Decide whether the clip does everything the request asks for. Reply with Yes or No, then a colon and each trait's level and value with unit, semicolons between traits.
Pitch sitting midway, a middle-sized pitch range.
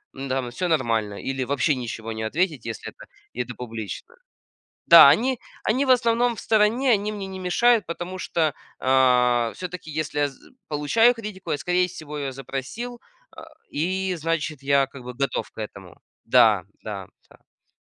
No: medium, 150 Hz; wide, 7.5 semitones